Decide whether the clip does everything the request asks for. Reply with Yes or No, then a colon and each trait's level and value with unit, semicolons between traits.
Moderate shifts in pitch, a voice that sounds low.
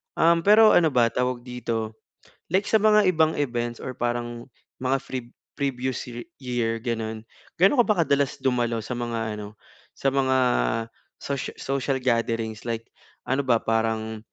Yes: average, 3.3 semitones; low, 125 Hz